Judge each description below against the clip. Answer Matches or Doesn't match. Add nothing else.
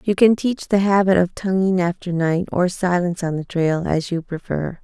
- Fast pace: Matches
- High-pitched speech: Doesn't match